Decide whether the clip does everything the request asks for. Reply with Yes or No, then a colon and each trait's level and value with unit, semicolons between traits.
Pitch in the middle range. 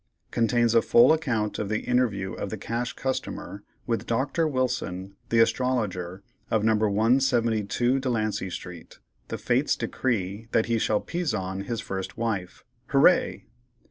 No: low, 115 Hz